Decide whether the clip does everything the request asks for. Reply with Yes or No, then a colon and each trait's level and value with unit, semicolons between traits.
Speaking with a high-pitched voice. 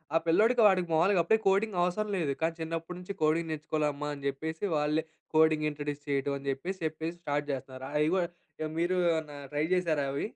No: medium, 160 Hz